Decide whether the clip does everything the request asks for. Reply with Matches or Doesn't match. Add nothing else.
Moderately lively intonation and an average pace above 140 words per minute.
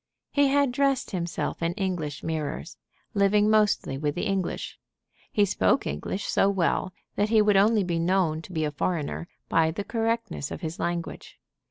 Matches